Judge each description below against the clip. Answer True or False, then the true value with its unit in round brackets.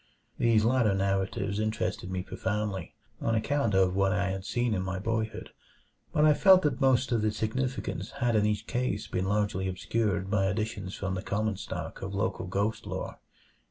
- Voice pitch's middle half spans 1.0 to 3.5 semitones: True (3.0 semitones)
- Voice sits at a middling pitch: False (105 Hz)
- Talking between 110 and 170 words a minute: False (180 wpm)